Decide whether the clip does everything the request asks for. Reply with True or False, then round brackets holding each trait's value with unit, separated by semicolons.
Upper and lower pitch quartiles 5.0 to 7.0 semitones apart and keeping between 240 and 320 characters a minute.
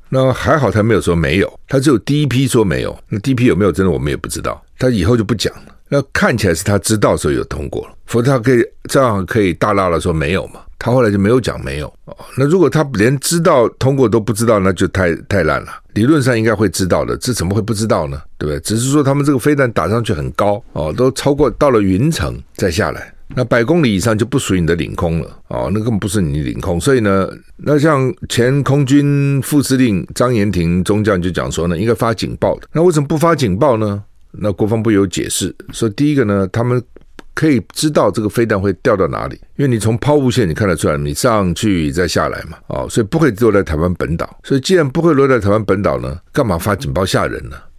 False (5.6 semitones; 355 characters per minute)